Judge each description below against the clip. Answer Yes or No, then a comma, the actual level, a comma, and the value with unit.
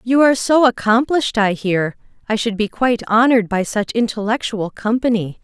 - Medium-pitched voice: No, high, 225 Hz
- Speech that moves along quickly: No, average, 165 wpm